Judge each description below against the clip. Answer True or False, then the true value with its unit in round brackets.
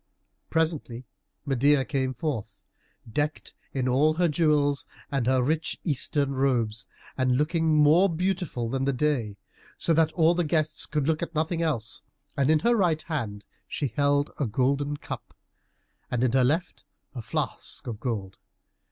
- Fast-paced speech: False (155 wpm)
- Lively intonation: False (3.8 semitones)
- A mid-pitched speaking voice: True (145 Hz)